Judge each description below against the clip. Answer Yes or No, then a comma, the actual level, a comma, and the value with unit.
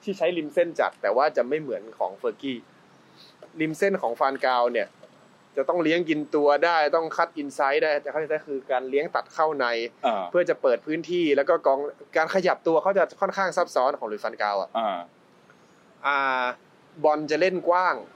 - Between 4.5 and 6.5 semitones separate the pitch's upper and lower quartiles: No, average, 3.8 semitones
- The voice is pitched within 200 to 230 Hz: No, medium, 155 Hz